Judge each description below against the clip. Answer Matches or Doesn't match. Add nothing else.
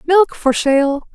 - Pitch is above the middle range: Matches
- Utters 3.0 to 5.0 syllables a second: Matches